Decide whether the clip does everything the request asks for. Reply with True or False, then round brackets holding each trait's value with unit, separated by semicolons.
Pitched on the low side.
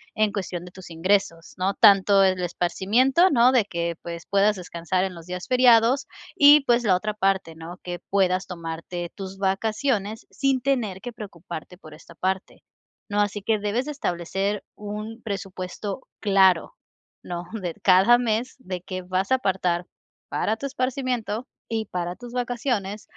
False (195 Hz)